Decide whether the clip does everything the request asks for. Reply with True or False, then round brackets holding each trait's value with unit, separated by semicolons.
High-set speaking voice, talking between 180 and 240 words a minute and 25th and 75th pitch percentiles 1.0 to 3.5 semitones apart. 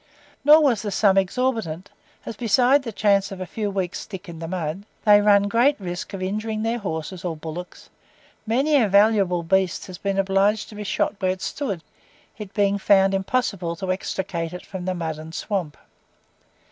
True (195 Hz; 185 wpm; 3.1 semitones)